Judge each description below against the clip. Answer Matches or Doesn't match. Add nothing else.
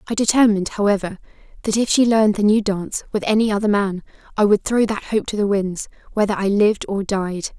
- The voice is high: Matches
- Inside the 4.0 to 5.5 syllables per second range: Doesn't match